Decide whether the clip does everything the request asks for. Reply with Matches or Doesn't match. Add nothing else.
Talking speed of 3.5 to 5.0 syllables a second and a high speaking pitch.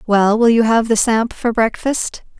Matches